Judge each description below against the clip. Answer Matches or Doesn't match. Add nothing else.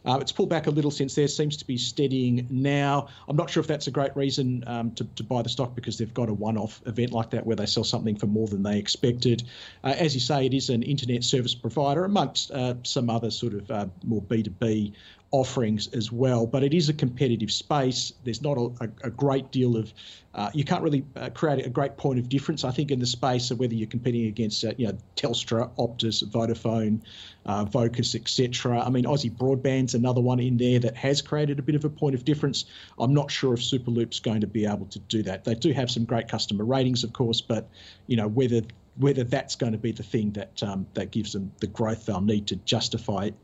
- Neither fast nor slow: Doesn't match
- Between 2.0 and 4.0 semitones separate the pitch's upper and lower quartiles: Matches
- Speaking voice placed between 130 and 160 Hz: Doesn't match